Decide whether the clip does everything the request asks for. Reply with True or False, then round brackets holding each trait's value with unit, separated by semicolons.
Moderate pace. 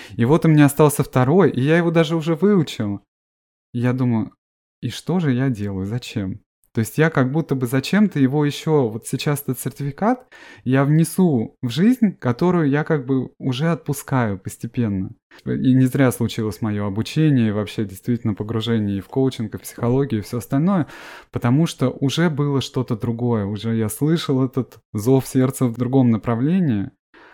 False (175 wpm)